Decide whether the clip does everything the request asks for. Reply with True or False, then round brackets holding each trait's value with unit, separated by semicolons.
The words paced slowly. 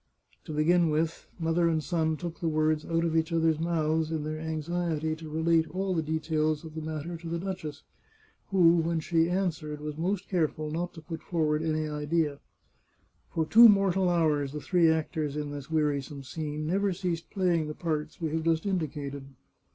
False (190 wpm)